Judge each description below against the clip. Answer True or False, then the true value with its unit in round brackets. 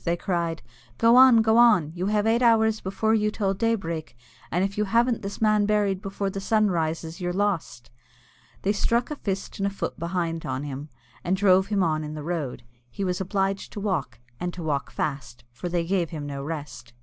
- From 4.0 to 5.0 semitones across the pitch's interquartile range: True (4.4 semitones)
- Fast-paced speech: True (210 wpm)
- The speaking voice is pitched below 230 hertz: True (190 Hz)